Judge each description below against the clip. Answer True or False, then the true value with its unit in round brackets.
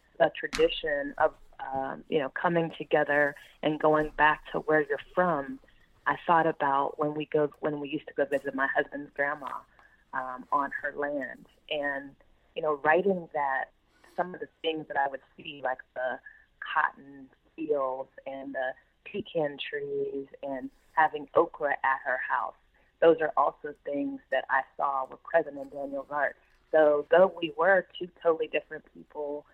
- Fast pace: False (165 wpm)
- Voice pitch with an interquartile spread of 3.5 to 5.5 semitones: False (2.5 semitones)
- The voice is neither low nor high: True (150 Hz)